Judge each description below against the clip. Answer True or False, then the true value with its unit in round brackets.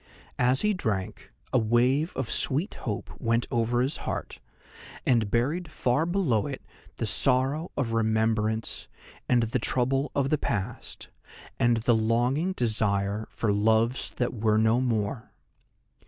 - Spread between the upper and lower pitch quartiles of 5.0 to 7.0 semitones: False (3.3 semitones)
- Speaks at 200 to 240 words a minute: False (140 wpm)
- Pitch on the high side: False (120 Hz)